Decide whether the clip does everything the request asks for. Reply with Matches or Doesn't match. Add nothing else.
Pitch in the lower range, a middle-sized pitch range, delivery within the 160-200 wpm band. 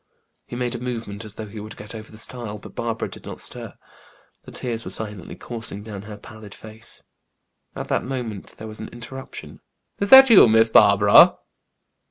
Doesn't match